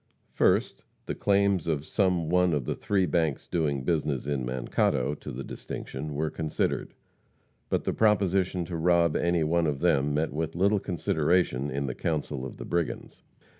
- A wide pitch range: No, average, 3.7 semitones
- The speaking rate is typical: Yes, average, 170 wpm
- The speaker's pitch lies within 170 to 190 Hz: No, very low, 80 Hz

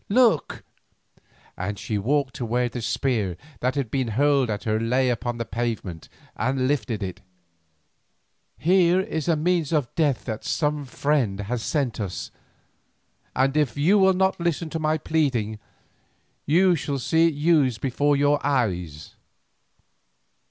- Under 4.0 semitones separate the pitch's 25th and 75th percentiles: No, average, 5.2 semitones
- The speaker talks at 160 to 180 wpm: No, average, 145 wpm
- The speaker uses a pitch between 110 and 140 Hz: Yes, low, 135 Hz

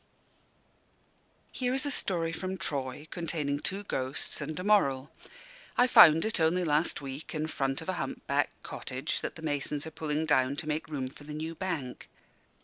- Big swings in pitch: No, average, 3.6 semitones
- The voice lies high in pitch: No, medium, 155 Hz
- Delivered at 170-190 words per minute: Yes, average, 180 wpm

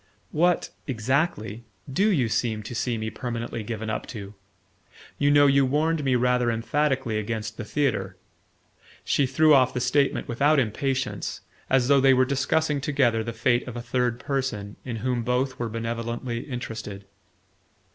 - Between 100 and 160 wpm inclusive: Yes, average, 155 wpm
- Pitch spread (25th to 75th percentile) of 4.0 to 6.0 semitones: No, average, 3.4 semitones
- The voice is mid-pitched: No, low, 125 Hz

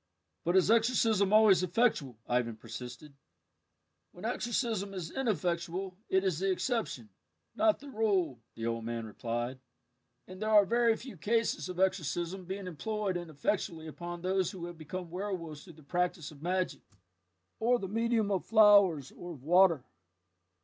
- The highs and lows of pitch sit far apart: No, average, 4.8 semitones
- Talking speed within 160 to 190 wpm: No, average, 150 wpm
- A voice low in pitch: No, medium, 185 Hz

